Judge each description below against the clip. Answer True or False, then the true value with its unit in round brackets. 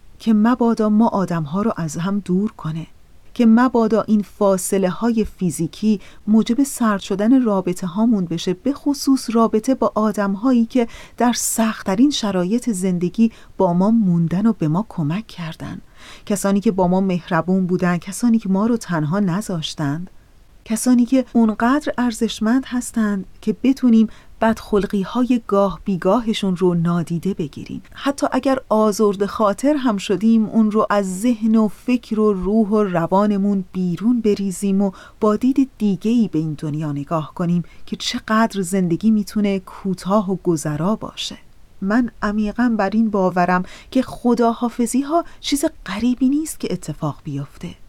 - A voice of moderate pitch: False (210 Hz)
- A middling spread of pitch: True (3.9 semitones)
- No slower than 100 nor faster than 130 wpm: False (150 wpm)